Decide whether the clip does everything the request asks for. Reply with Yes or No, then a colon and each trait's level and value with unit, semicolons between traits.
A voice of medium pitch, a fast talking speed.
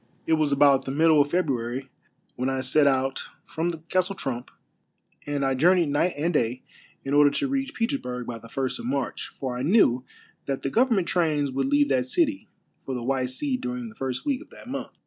Yes: medium, 145 Hz; fast, 215 wpm